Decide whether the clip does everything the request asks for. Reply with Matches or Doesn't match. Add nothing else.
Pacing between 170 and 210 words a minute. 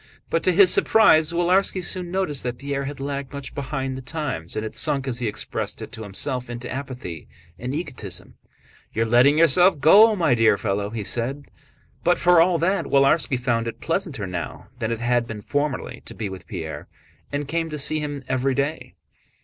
Matches